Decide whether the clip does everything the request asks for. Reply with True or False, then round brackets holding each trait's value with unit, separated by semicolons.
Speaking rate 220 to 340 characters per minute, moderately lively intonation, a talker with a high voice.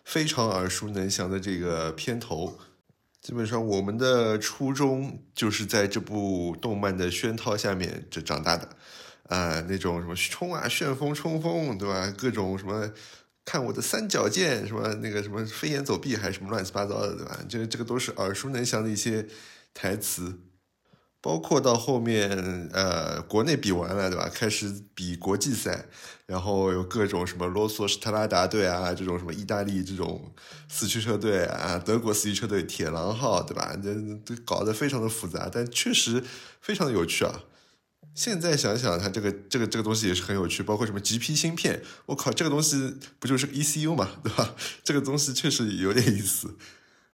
False (280 characters per minute; 4.6 semitones; 105 Hz)